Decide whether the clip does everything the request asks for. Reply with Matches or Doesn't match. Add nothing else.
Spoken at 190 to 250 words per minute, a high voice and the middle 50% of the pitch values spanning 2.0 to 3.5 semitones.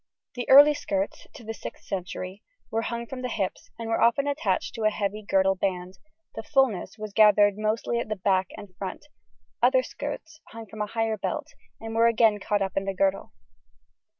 Matches